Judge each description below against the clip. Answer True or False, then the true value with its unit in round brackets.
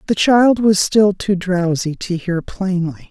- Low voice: False (190 Hz)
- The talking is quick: False (175 wpm)